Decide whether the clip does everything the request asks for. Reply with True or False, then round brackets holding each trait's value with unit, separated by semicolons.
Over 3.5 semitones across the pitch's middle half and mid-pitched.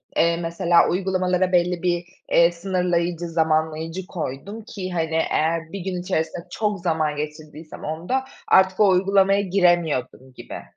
False (2.6 semitones; 175 Hz)